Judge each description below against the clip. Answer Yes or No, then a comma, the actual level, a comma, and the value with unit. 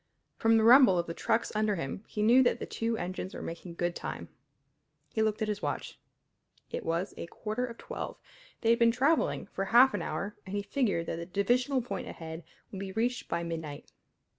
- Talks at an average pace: No, fast, 210 wpm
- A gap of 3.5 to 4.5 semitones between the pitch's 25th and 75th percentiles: No, average, 5.1 semitones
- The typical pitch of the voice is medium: No, high, 210 Hz